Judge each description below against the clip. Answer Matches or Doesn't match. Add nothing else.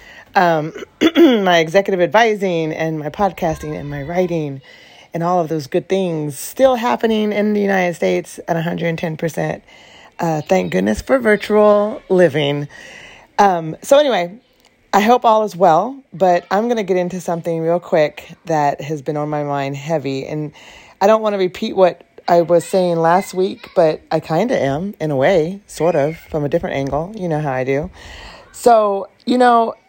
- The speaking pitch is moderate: Matches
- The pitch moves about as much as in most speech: Matches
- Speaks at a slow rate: Doesn't match